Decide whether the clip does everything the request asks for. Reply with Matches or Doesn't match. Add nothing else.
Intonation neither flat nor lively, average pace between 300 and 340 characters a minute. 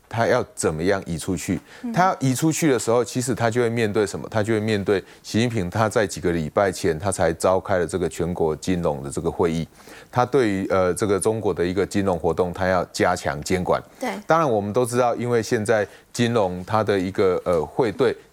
Matches